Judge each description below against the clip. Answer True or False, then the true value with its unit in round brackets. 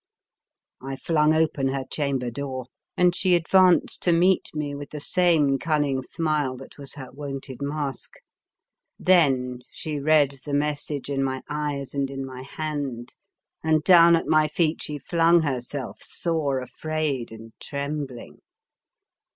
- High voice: False (145 Hz)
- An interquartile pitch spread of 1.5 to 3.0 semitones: True (2.6 semitones)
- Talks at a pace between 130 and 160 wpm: True (145 wpm)